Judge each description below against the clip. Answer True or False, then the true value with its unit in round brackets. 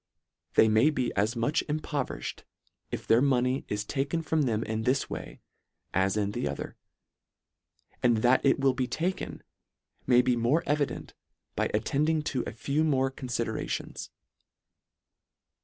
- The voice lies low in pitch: True (130 Hz)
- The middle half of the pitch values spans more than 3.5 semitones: True (4.3 semitones)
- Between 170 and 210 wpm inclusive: False (150 wpm)